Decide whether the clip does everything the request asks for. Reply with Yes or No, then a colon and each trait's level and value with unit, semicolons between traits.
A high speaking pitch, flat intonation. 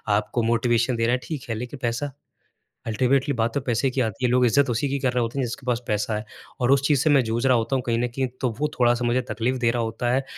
No: low, 125 Hz; narrow, 2.1 semitones